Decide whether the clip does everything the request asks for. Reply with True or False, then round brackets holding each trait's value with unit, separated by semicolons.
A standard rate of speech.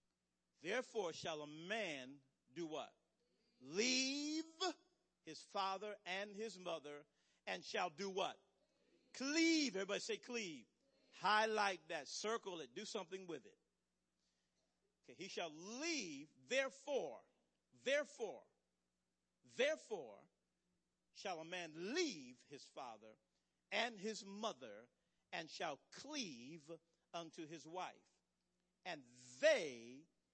False (105 wpm)